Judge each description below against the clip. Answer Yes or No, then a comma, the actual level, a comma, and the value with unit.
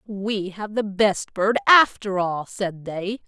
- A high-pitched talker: Yes, high, 200 Hz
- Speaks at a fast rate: No, average, 165 wpm